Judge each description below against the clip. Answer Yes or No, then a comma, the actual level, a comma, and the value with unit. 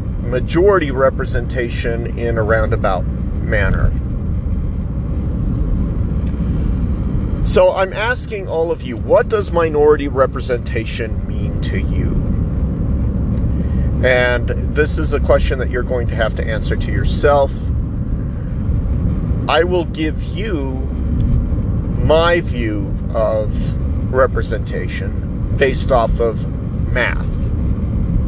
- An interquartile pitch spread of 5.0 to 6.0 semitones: Yes, wide, 5.5 semitones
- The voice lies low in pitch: Yes, low, 110 Hz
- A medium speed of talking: No, slow, 95 wpm